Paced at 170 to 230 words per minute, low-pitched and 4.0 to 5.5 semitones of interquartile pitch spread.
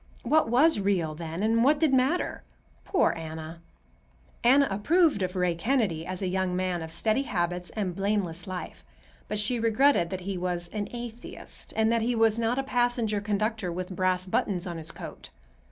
No: average, 180 wpm; high, 200 Hz; average, 4.8 semitones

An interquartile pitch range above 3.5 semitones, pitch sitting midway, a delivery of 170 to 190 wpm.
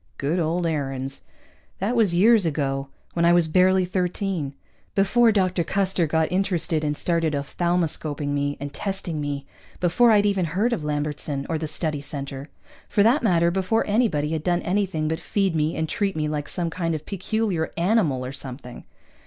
Yes: average, 4.4 semitones; medium, 170 Hz; average, 180 wpm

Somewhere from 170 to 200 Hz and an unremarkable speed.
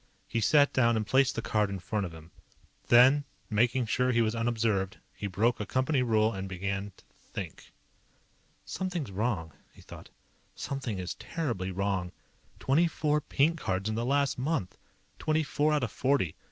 No: low, 115 Hz; average, 170 wpm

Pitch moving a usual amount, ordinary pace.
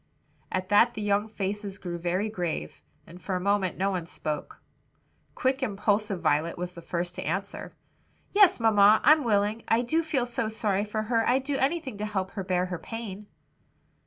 Yes: average, 3.6 semitones; average, 185 wpm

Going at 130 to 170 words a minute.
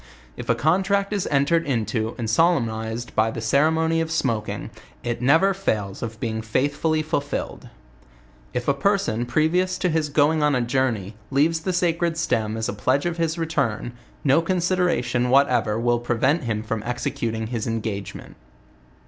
Yes: average, 160 wpm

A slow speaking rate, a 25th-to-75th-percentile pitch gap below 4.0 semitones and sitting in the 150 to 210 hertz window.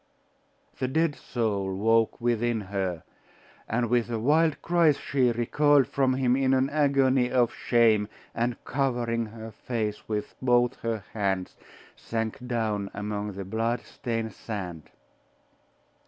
No: slow, 130 wpm; average, 3.4 semitones; low, 115 Hz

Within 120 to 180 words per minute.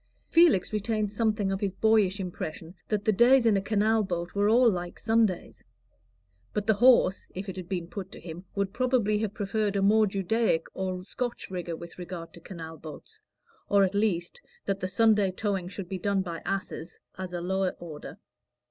No: average, 190 wpm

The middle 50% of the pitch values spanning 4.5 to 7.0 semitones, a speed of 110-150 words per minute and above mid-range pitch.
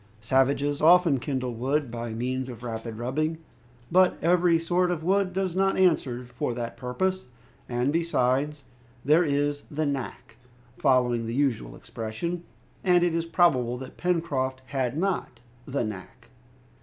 No: wide, 5.4 semitones; average, 145 wpm; medium, 140 Hz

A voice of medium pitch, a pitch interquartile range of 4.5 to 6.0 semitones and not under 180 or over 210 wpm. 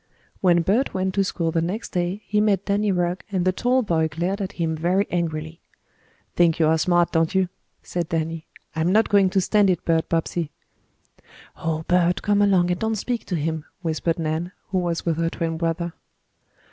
No: medium, 175 Hz; average, 2.8 semitones; average, 195 wpm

